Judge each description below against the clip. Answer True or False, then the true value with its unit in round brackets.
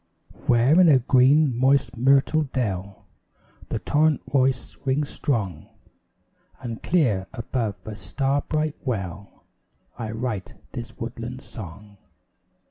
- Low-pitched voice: True (125 Hz)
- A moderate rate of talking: False (115 wpm)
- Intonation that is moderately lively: True (4.5 semitones)